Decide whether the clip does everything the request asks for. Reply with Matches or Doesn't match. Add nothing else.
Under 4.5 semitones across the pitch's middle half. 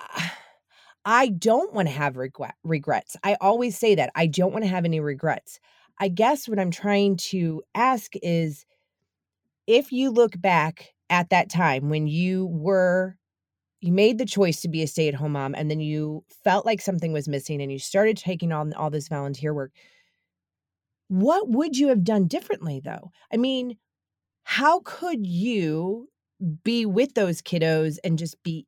Doesn't match